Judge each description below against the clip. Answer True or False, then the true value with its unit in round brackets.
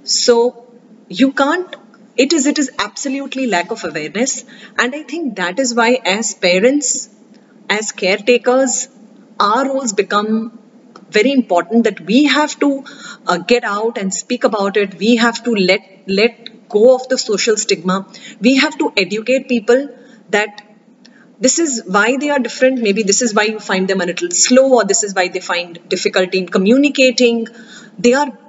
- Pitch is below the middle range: False (230 Hz)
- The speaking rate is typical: True (170 wpm)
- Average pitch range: True (3.8 semitones)